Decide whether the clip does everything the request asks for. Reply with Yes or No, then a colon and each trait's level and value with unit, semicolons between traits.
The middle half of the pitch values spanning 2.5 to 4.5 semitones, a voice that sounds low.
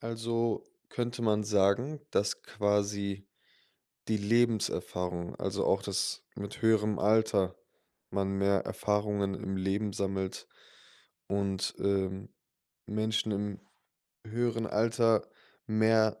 No: narrow, 2.1 semitones; low, 105 Hz